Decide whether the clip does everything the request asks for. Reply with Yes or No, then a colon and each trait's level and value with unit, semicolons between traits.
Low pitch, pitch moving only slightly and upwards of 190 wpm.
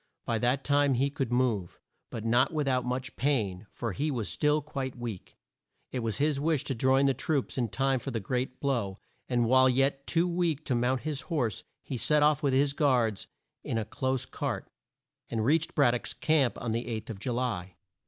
No: low, 130 Hz; average, 3.3 semitones; fast, 205 wpm